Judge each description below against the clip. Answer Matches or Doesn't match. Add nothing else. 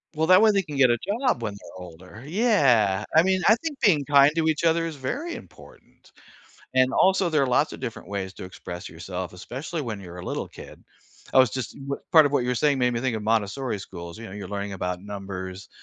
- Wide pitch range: Matches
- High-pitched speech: Doesn't match